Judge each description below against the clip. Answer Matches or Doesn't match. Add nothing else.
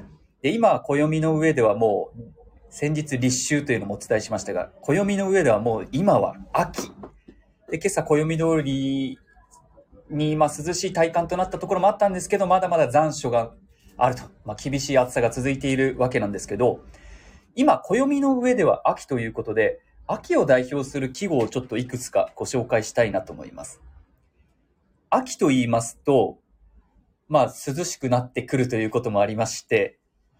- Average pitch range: Doesn't match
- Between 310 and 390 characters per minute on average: Matches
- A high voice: Doesn't match